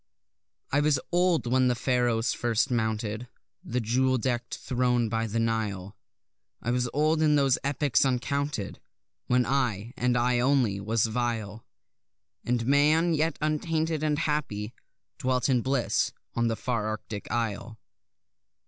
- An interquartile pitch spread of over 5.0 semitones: No, average, 3.7 semitones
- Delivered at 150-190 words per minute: No, average, 140 wpm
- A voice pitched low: Yes, low, 125 Hz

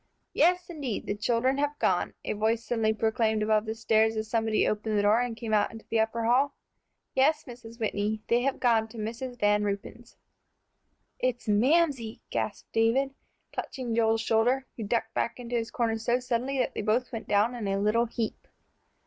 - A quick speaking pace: No, average, 185 wpm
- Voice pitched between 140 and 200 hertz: No, high, 225 Hz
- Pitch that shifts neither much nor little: No, narrow, 2.1 semitones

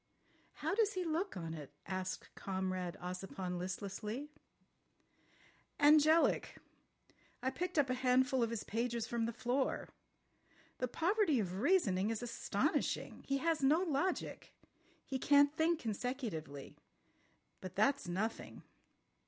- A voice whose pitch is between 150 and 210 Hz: No, high, 245 Hz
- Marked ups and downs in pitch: Yes, wide, 7.5 semitones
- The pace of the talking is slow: Yes, slow, 120 wpm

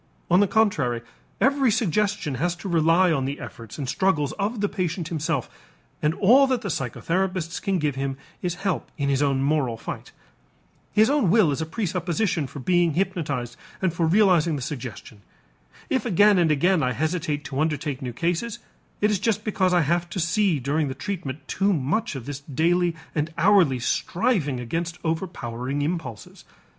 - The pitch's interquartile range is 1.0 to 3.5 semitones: No, average, 5.2 semitones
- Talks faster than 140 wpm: Yes, average, 170 wpm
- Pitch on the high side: No, medium, 165 Hz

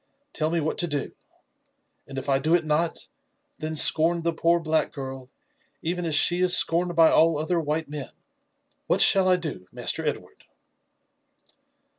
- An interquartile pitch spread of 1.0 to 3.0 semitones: Yes, narrow, 2.4 semitones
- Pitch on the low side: No, medium, 160 Hz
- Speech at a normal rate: Yes, average, 170 wpm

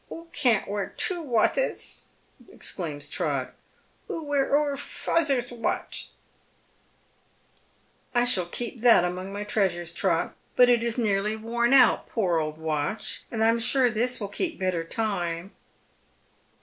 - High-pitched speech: Yes, high, 225 Hz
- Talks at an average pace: Yes, average, 150 wpm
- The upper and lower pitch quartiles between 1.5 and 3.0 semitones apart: No, average, 5.2 semitones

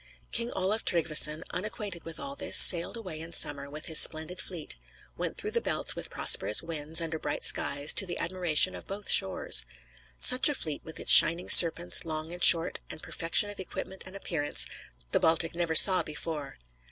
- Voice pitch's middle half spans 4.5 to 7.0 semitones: No, average, 3.1 semitones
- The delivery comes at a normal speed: Yes, average, 190 wpm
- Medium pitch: Yes, medium, 165 Hz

